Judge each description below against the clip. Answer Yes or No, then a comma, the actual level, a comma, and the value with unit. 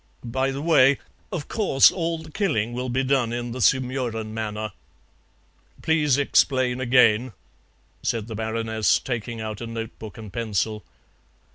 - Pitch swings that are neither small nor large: Yes, average, 3.2 semitones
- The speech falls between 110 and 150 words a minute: Yes, average, 140 wpm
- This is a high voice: No, low, 120 Hz